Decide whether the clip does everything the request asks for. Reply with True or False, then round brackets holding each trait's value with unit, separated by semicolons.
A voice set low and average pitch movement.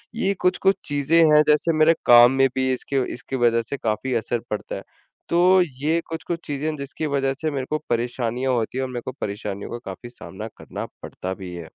True (130 Hz; 4.5 semitones)